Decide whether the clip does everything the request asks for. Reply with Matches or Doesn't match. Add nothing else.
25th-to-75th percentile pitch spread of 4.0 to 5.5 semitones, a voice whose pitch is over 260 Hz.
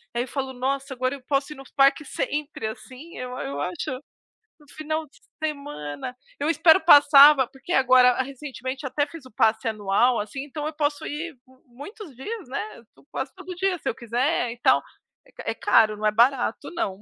Doesn't match